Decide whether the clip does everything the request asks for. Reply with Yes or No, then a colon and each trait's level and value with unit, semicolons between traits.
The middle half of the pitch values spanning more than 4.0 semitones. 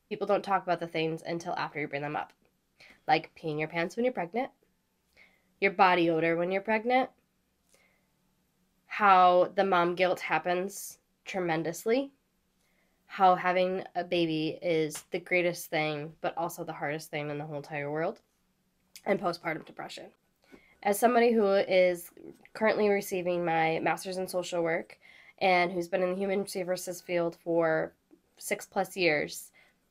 No: average, 2.9 semitones